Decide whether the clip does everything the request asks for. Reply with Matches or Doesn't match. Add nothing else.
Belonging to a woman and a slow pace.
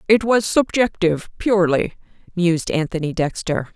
Matches